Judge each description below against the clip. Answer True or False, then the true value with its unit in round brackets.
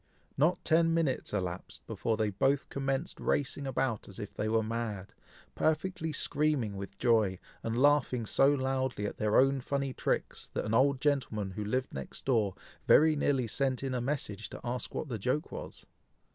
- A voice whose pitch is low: True (130 Hz)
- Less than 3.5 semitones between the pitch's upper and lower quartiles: False (4.6 semitones)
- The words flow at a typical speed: True (175 wpm)